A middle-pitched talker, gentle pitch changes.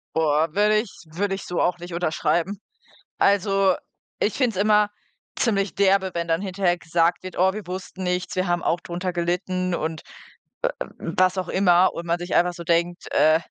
Yes: medium, 180 Hz; narrow, 2.1 semitones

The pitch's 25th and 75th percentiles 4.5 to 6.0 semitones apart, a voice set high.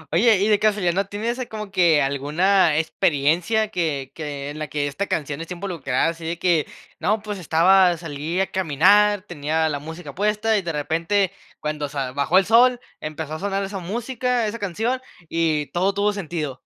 No: average, 5.0 semitones; medium, 175 Hz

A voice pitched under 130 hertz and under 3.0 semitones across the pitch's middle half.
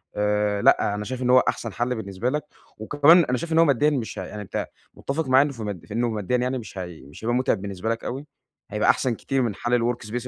No: low, 120 Hz; average, 3.8 semitones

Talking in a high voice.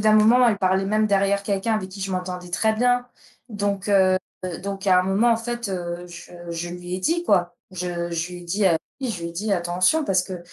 Yes: high, 195 Hz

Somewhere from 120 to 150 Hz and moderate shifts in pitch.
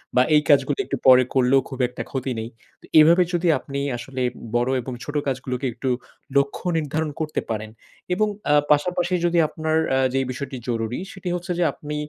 Yes: medium, 140 Hz; average, 3.6 semitones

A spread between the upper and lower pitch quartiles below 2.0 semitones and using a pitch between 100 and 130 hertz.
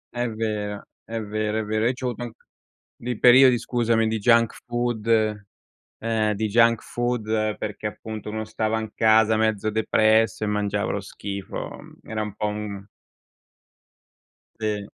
Yes: narrow, 1.5 semitones; low, 110 Hz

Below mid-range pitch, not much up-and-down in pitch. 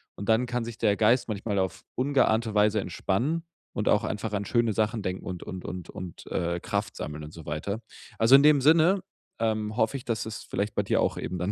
No: low, 110 Hz; average, 3.8 semitones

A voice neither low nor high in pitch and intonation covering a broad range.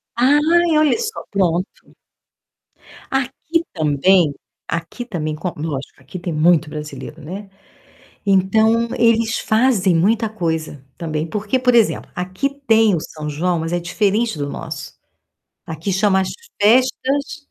No: high, 195 Hz; wide, 6.2 semitones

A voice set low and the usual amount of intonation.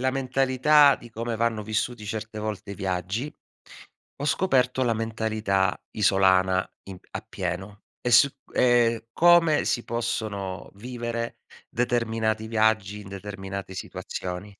Yes: low, 110 Hz; average, 3.6 semitones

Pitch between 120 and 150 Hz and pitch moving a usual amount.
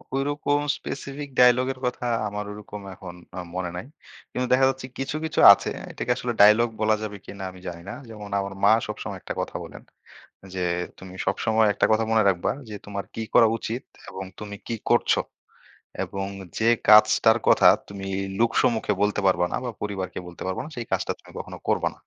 No: low, 110 Hz; average, 3.7 semitones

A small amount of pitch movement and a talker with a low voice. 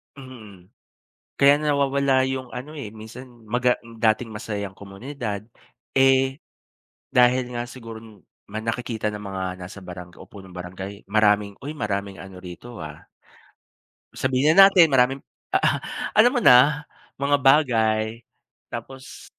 No: average, 4.7 semitones; low, 115 Hz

